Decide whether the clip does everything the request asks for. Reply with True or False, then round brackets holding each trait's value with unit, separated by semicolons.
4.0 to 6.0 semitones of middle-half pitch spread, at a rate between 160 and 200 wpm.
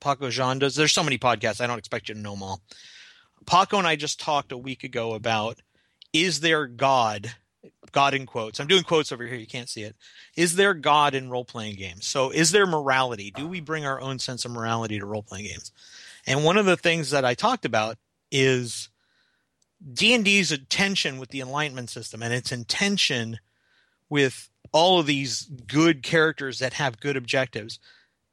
True (4.8 semitones; 190 wpm)